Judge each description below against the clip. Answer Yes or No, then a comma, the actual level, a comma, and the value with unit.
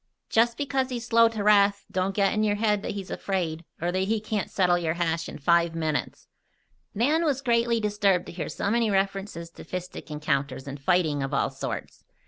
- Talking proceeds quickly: Yes, fast, 210 wpm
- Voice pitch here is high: Yes, high, 195 Hz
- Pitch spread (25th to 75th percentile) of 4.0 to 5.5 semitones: Yes, average, 4.6 semitones